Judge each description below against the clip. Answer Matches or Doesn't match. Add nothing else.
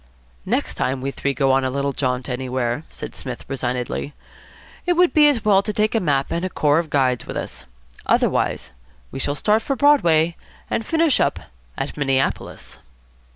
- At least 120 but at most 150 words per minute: Doesn't match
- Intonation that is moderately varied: Doesn't match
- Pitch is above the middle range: Doesn't match